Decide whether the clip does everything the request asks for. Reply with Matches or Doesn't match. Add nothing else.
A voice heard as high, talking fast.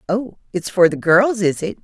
Matches